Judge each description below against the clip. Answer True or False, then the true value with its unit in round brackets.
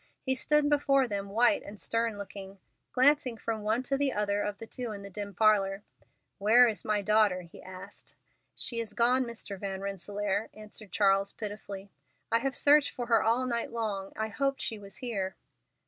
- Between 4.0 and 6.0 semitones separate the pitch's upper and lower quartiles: False (3.3 semitones)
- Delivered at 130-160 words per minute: False (185 wpm)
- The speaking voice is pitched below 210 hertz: False (215 Hz)